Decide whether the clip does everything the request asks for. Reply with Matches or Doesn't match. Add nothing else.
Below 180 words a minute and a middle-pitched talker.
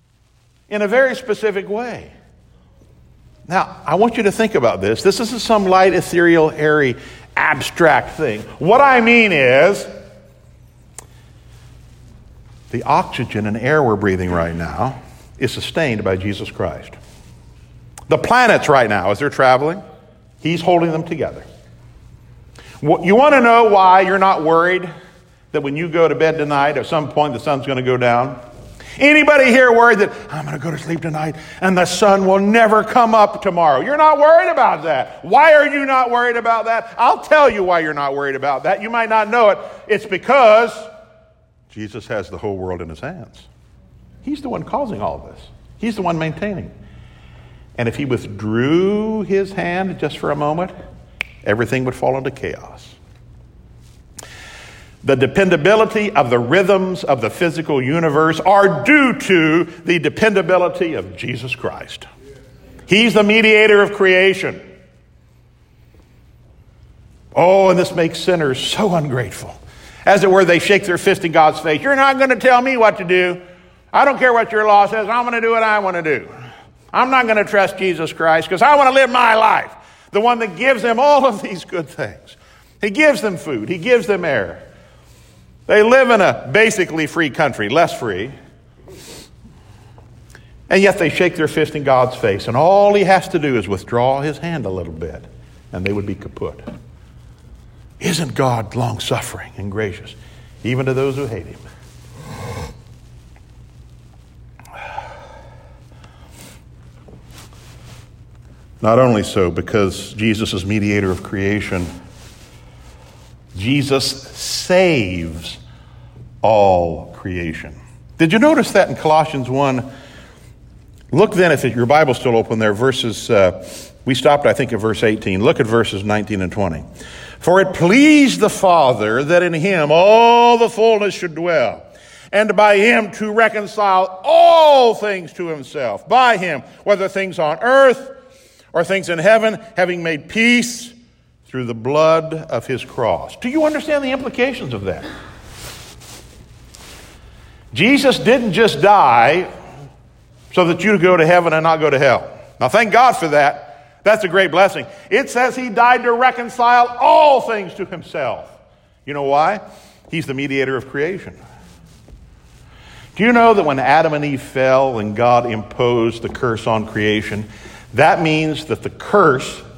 Matches